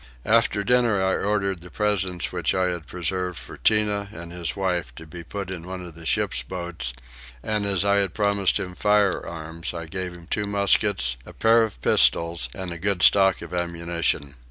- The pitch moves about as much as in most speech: Yes, average, 3.0 semitones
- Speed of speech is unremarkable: Yes, average, 190 wpm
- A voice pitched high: No, very low, 90 Hz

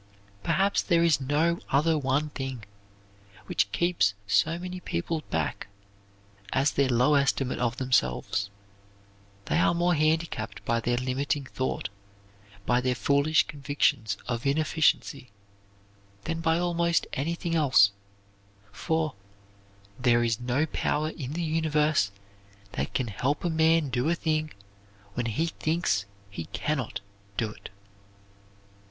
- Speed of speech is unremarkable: No, slow, 130 wpm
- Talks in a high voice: No, medium, 145 Hz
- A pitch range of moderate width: Yes, average, 4.6 semitones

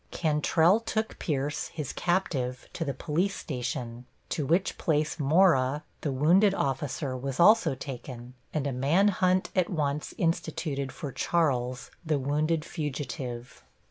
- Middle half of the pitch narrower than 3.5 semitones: No, average, 4.2 semitones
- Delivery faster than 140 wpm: No, slow, 135 wpm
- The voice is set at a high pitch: No, medium, 150 Hz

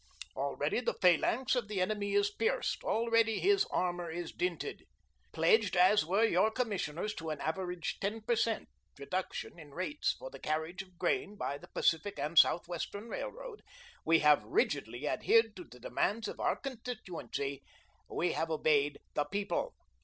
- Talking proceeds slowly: No, average, 160 wpm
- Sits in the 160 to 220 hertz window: Yes, high, 190 Hz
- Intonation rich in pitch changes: Yes, wide, 5.7 semitones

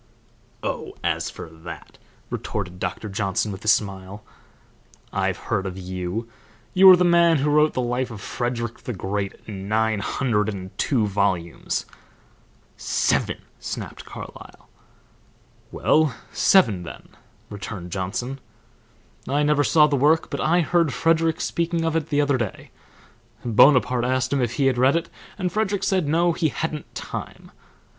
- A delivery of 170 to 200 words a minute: No, average, 150 wpm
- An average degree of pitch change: No, wide, 7.6 semitones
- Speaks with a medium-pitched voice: No, low, 125 Hz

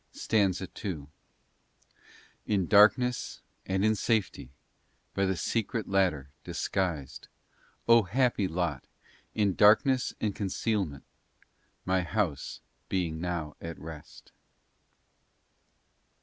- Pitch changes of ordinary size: Yes, average, 4.3 semitones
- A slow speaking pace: Yes, slow, 90 wpm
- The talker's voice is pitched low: Yes, very low, 95 Hz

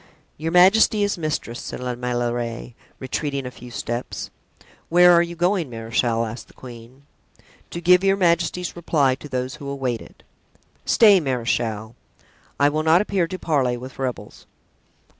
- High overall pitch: No, medium, 140 Hz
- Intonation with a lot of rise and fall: Yes, wide, 5.9 semitones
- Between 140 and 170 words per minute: Yes, average, 155 wpm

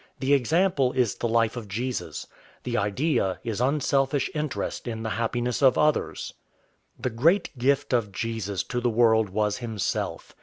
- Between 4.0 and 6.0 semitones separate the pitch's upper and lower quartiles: No, average, 3.6 semitones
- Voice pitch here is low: Yes, low, 120 Hz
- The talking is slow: No, average, 155 wpm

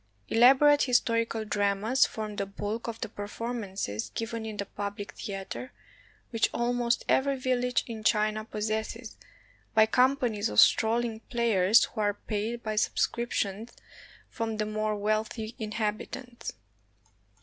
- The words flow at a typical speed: No, slow, 125 wpm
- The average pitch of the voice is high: Yes, high, 220 Hz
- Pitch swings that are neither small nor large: No, narrow, 2.1 semitones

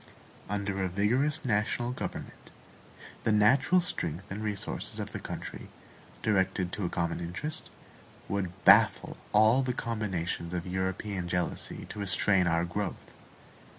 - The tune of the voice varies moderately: Yes, average, 3.4 semitones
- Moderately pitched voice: No, low, 100 Hz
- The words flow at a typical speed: No, slow, 130 wpm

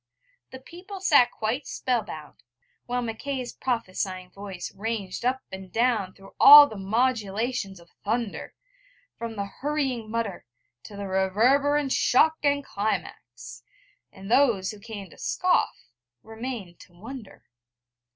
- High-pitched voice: Yes, high, 225 Hz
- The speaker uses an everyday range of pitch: Yes, average, 5.0 semitones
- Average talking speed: No, slow, 130 wpm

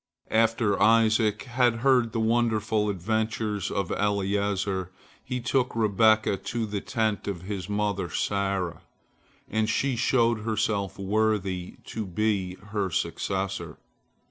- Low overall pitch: Yes, low, 105 Hz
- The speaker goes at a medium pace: No, slow, 115 wpm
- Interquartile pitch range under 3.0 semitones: Yes, narrow, 2.4 semitones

